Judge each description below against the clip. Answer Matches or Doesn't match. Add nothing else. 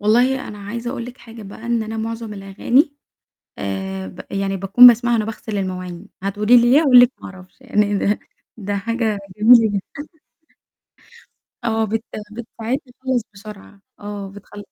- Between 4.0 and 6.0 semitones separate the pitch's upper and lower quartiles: Doesn't match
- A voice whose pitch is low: Doesn't match